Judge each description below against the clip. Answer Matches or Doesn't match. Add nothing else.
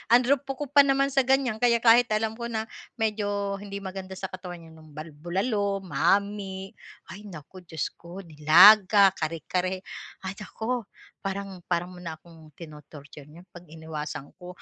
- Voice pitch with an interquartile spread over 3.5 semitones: Matches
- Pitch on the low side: Doesn't match